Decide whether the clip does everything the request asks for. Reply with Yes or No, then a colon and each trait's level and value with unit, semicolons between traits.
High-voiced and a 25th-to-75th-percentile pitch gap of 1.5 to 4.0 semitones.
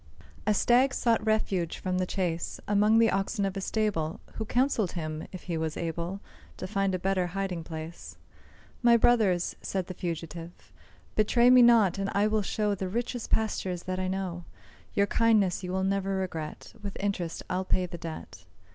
Yes: high, 195 Hz; average, 3.4 semitones